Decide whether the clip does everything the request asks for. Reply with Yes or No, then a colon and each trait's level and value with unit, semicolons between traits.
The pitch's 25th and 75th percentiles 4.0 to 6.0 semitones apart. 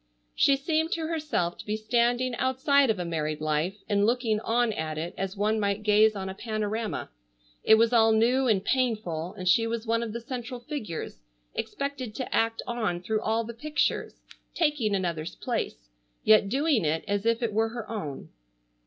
No: average, 3.6 semitones